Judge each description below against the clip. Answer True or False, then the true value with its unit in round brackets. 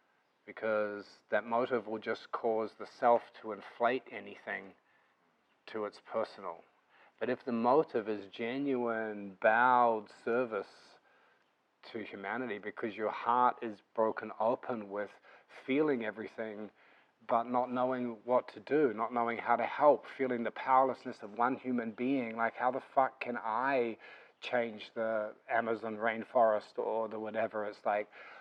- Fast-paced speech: False (140 wpm)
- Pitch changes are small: True (2.2 semitones)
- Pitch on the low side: True (115 Hz)